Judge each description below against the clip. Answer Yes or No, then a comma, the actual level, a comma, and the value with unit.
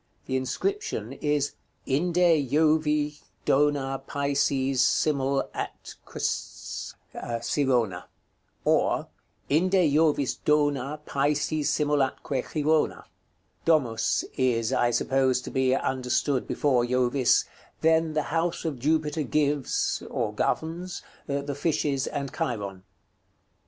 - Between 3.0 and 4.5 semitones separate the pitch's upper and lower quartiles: No, narrow, 2.6 semitones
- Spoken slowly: Yes, slow, 100 wpm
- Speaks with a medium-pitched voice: Yes, medium, 145 Hz